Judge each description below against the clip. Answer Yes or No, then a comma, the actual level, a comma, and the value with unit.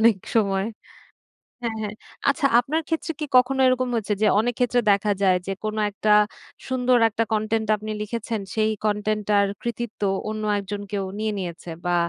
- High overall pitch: Yes, high, 215 Hz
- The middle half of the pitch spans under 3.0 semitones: Yes, narrow, 2.6 semitones